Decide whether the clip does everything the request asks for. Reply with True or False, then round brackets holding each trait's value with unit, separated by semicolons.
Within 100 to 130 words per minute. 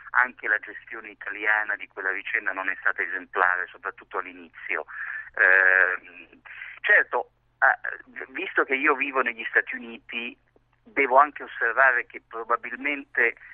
True (120 wpm)